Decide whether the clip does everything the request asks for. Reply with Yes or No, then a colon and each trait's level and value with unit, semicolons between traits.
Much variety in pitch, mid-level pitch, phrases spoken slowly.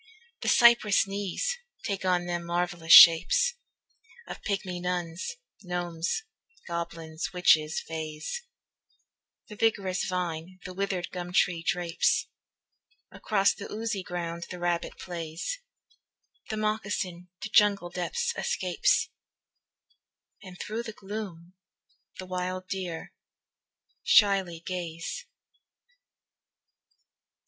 No: average, 2.8 semitones; medium, 180 Hz; slow, 100 wpm